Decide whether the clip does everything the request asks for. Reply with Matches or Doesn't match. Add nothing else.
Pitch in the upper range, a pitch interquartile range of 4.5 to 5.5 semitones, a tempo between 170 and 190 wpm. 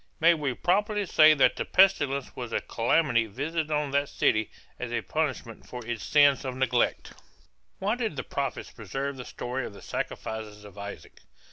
Doesn't match